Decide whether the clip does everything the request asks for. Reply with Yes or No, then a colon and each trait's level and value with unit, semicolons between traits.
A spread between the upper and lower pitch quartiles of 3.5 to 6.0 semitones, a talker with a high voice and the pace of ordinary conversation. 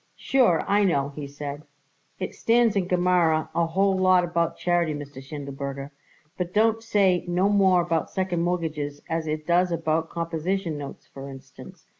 No: average, 3.9 semitones; medium, 170 Hz; average, 165 wpm